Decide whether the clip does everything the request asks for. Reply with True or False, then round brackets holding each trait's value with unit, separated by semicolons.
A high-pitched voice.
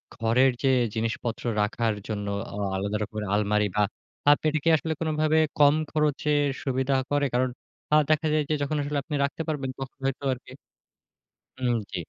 False (135 Hz)